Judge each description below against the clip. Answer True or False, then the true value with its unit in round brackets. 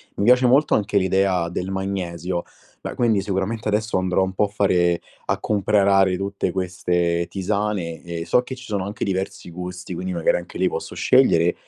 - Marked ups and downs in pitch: False (2.8 semitones)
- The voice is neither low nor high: False (95 Hz)